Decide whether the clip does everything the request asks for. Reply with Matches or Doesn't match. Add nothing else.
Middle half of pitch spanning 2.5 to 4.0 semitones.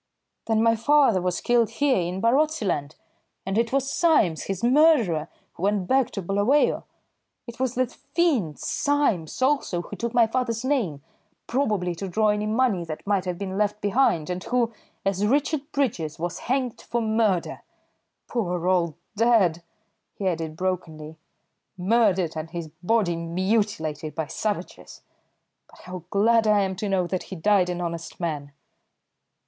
Doesn't match